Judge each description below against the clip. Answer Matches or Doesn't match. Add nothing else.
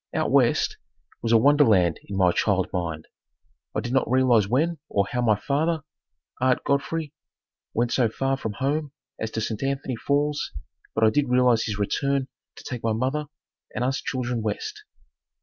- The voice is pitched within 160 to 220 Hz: Doesn't match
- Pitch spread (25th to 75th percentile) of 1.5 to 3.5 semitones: Doesn't match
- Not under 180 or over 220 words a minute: Doesn't match